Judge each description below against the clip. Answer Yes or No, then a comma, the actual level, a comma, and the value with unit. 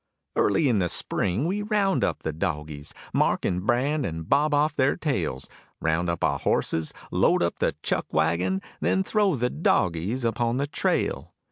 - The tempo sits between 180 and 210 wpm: No, average, 170 wpm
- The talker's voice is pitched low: Yes, low, 100 Hz